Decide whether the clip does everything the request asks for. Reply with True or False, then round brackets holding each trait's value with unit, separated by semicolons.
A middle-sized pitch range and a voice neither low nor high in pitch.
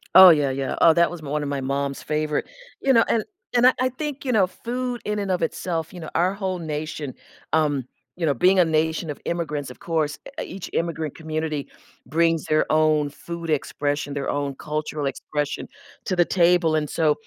True (3.4 semitones; 160 Hz)